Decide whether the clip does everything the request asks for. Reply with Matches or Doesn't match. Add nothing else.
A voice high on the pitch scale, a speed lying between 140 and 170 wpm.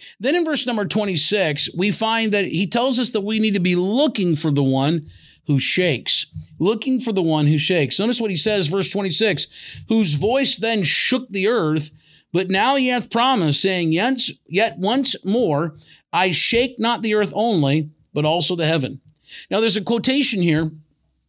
Doesn't match